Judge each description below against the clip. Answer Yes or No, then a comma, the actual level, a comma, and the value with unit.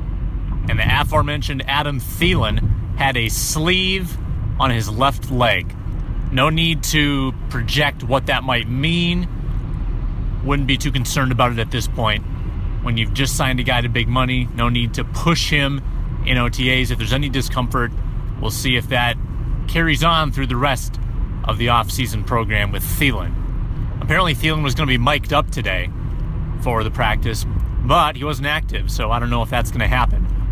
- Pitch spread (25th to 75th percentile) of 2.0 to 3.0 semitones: No, average, 3.7 semitones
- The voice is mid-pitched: No, low, 120 Hz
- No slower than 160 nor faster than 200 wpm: Yes, average, 175 wpm